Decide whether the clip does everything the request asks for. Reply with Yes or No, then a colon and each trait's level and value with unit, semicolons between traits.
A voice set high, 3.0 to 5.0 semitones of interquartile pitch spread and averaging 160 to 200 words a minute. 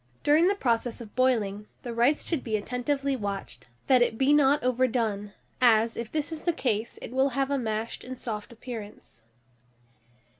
Yes: high, 245 Hz; average, 3.7 semitones; average, 175 wpm